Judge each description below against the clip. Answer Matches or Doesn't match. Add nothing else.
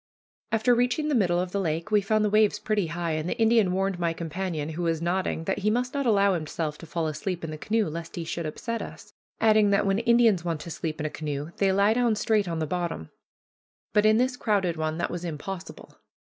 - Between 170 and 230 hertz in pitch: Matches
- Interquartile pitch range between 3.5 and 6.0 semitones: Matches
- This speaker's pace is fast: Matches